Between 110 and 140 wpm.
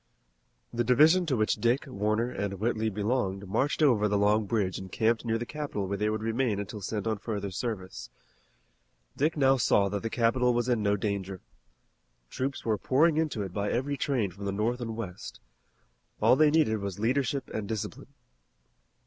No: average, 185 wpm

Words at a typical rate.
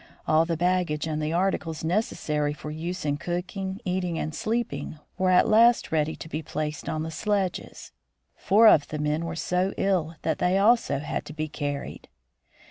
Yes: average, 180 wpm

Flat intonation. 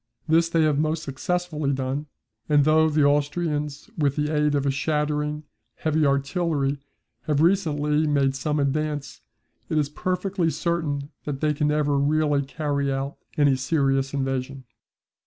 Yes: narrow, 1.8 semitones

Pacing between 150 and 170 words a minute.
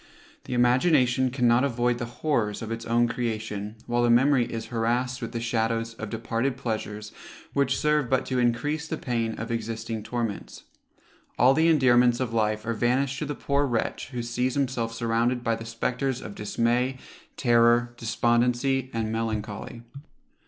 Yes: average, 160 wpm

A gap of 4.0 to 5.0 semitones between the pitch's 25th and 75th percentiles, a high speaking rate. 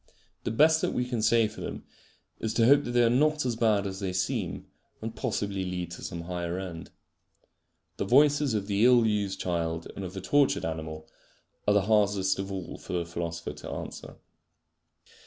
No: average, 4.7 semitones; average, 195 wpm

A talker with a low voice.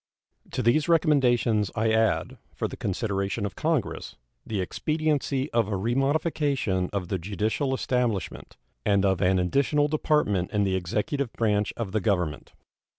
Yes: low, 110 Hz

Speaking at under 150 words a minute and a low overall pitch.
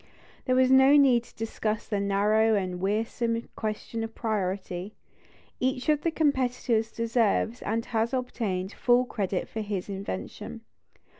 No: average, 140 wpm; high, 225 Hz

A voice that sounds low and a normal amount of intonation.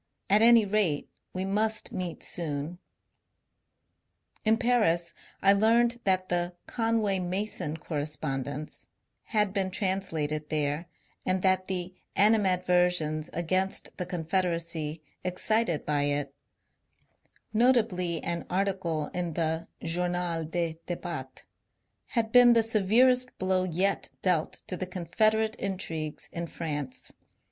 No: medium, 180 Hz; average, 4.0 semitones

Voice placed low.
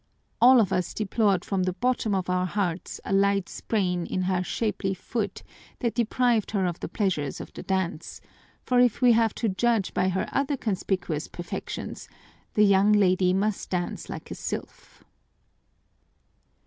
No: high, 195 Hz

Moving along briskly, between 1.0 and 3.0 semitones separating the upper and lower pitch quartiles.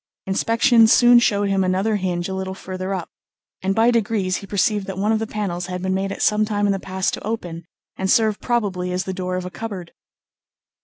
Yes: fast, 220 wpm; narrow, 2.6 semitones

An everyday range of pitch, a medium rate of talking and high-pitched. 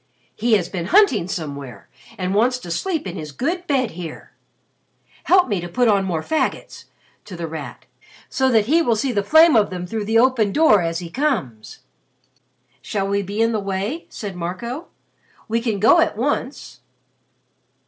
No: wide, 6.3 semitones; average, 180 wpm; high, 210 Hz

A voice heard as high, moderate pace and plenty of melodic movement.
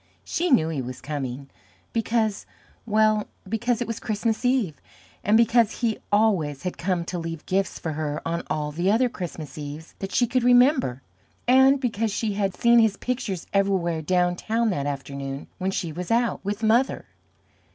Yes: high, 195 Hz; average, 170 wpm; wide, 6.1 semitones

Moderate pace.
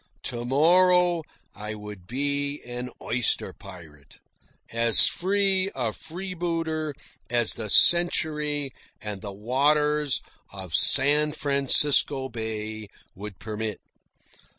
No: slow, 100 wpm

